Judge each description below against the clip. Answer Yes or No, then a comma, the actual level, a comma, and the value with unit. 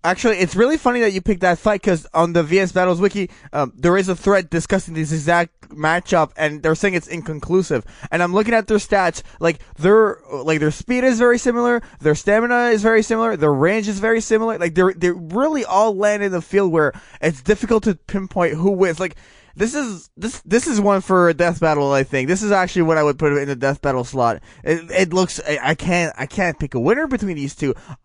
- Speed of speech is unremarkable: No, fast, 230 wpm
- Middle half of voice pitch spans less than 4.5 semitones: No, average, 5.1 semitones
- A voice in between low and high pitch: Yes, medium, 180 Hz